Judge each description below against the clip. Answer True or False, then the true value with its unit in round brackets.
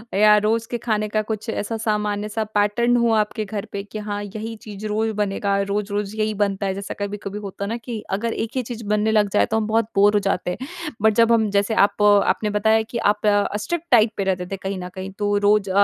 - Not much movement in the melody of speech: True (1.5 semitones)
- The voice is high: True (210 Hz)